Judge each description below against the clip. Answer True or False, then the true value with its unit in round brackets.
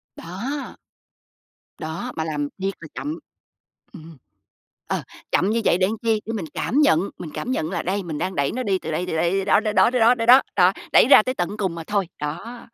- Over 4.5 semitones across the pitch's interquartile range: True (5.5 semitones)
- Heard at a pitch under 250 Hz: True (195 Hz)